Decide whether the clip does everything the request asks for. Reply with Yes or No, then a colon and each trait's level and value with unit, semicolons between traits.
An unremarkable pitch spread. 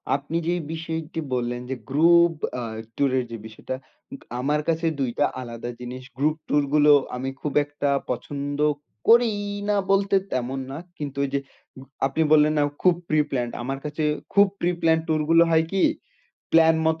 Yes: average, 3.6 semitones